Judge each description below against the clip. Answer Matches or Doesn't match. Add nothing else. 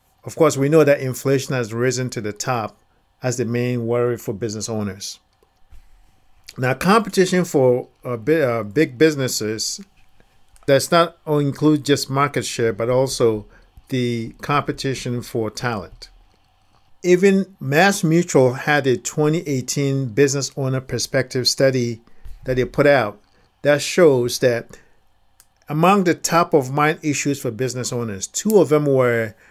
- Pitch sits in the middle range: Doesn't match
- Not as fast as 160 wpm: Matches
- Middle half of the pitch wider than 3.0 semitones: Matches